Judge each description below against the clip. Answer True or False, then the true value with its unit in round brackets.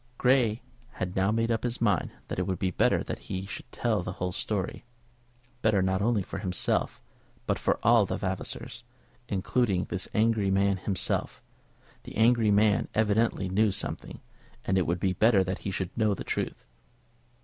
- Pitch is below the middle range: True (100 Hz)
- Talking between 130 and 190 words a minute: True (175 wpm)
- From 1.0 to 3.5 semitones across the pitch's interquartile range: True (2.8 semitones)